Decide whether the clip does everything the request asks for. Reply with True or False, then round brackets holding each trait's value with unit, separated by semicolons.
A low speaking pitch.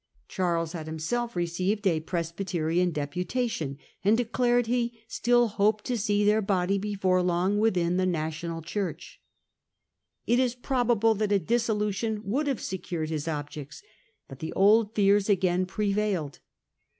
False (195 Hz)